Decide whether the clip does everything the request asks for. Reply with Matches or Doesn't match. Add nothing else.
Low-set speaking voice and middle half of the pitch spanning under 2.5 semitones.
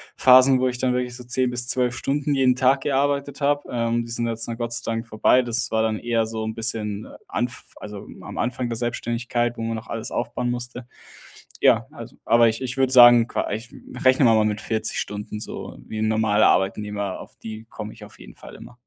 Matches